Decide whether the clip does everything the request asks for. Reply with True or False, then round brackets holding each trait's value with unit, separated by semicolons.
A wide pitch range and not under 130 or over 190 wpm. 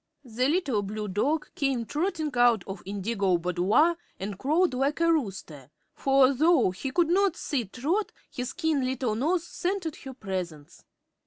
True (7.8 semitones; 155 wpm)